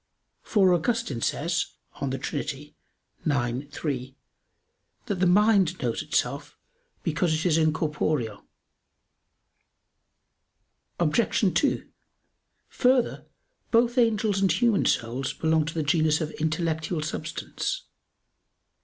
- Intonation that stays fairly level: No, average, 5.1 semitones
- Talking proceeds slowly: Yes, slow, 100 wpm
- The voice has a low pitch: No, medium, 165 Hz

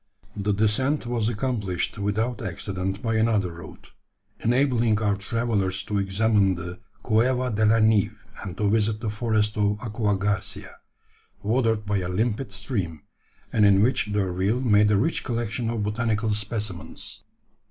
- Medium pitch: No, low, 105 Hz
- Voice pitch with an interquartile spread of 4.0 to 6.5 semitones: No, narrow, 2.4 semitones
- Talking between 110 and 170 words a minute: Yes, average, 145 wpm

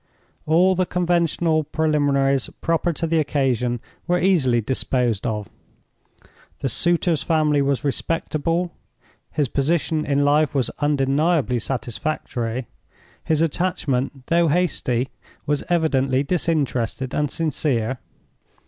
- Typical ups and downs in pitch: Yes, average, 3.9 semitones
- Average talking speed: No, slow, 105 wpm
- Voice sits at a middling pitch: Yes, medium, 145 Hz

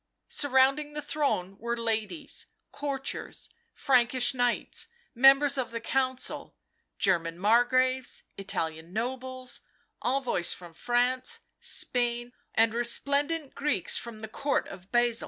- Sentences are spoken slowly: Yes, slow, 110 wpm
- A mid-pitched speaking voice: No, high, 245 Hz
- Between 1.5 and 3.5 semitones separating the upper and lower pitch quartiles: Yes, average, 3.1 semitones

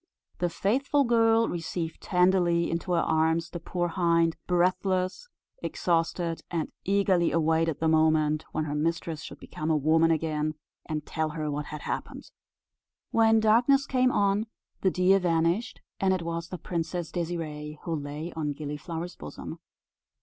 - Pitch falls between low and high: Yes, medium, 170 Hz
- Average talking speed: Yes, average, 150 wpm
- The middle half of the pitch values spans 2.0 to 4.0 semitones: Yes, average, 2.8 semitones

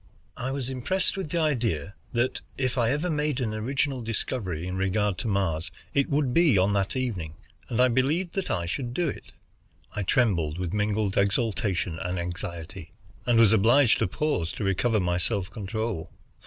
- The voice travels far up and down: Yes, wide, 5.9 semitones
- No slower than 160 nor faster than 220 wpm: Yes, average, 180 wpm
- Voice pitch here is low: Yes, low, 110 Hz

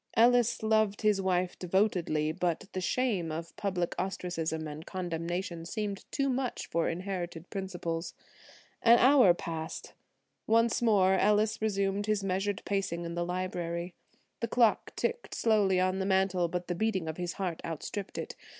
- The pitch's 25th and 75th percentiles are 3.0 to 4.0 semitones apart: Yes, average, 3.5 semitones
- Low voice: No, high, 190 Hz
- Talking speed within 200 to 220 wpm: No, average, 150 wpm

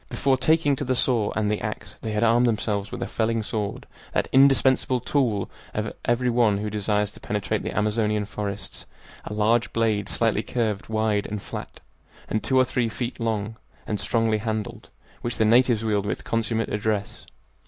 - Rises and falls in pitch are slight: Yes, narrow, 2.2 semitones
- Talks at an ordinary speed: Yes, average, 180 wpm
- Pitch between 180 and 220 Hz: No, low, 110 Hz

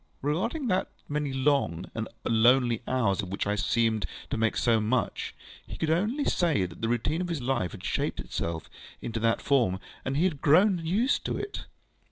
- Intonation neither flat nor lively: No, wide, 6.7 semitones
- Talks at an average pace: Yes, average, 190 wpm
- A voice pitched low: Yes, low, 130 Hz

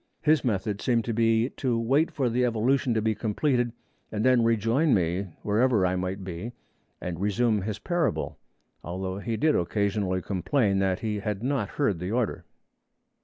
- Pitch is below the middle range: Yes, low, 110 Hz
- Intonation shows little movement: No, average, 4.0 semitones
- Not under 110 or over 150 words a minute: No, average, 170 wpm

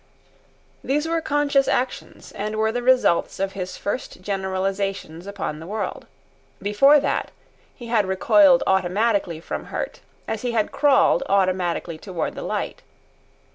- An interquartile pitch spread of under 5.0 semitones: No, average, 5.3 semitones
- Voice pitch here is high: Yes, high, 205 Hz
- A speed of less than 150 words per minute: Yes, slow, 135 wpm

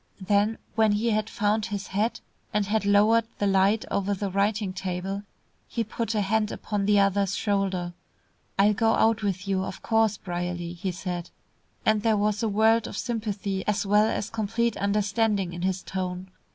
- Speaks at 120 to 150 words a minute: No, average, 180 wpm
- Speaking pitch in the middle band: No, high, 205 Hz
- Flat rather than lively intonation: Yes, narrow, 2.2 semitones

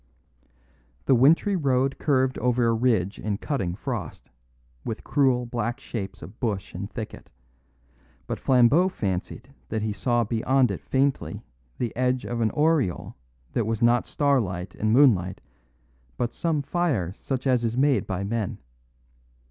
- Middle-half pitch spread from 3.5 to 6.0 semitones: Yes, average, 4.0 semitones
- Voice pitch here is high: No, low, 120 Hz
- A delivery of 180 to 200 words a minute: No, average, 145 wpm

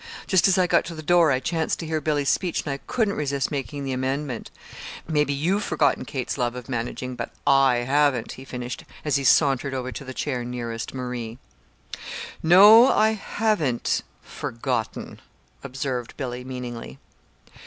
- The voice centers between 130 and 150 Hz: Yes, low, 135 Hz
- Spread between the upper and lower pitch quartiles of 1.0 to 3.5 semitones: No, average, 3.9 semitones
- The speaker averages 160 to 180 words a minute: Yes, average, 165 wpm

